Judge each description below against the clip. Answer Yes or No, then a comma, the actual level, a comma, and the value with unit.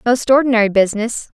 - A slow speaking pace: Yes, slow, 130 wpm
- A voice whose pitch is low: No, high, 230 Hz